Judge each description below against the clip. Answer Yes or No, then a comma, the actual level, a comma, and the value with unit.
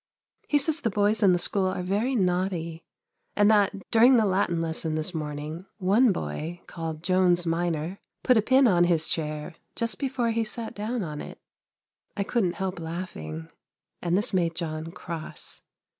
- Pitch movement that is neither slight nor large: Yes, average, 4.6 semitones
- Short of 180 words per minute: Yes, average, 170 wpm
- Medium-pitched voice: Yes, medium, 180 Hz